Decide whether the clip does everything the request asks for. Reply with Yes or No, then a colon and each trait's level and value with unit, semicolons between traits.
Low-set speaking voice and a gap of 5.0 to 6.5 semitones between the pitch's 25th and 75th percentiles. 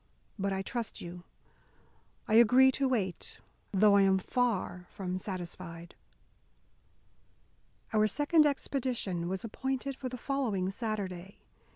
No: high, 205 Hz; average, 5.3 semitones